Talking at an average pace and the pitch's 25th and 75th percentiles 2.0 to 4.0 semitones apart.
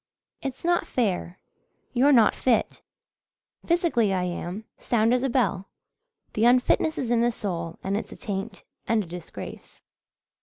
No: average, 150 wpm; average, 4.6 semitones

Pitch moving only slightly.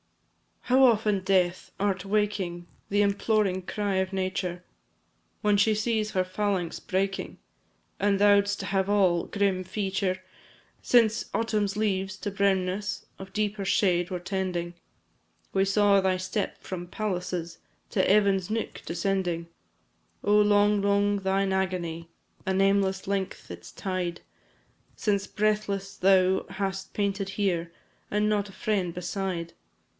Yes: narrow, 1.8 semitones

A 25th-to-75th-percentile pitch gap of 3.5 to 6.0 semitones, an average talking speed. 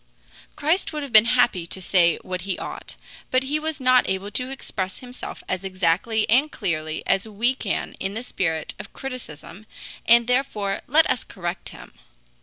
Yes: wide, 5.4 semitones; average, 175 wpm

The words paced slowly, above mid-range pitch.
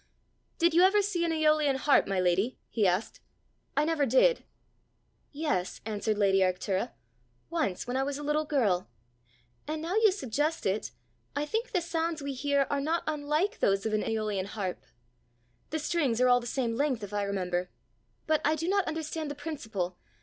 No: average, 185 wpm; very high, 280 Hz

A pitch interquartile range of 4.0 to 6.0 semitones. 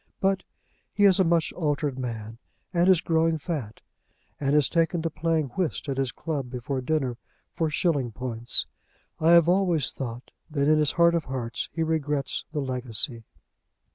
Yes: average, 4.4 semitones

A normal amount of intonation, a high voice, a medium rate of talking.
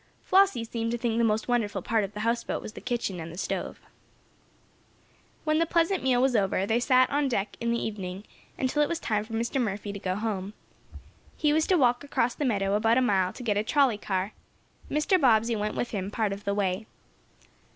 No: average, 4.0 semitones; high, 225 Hz; fast, 215 wpm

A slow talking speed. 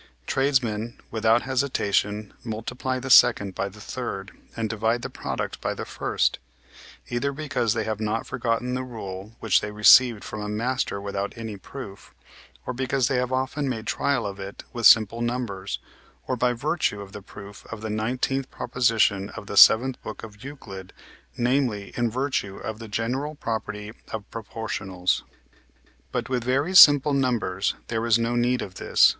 No: average, 165 wpm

